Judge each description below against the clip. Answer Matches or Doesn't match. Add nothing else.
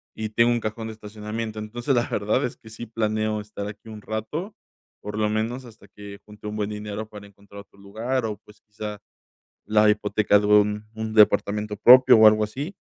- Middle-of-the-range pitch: Doesn't match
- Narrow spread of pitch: Matches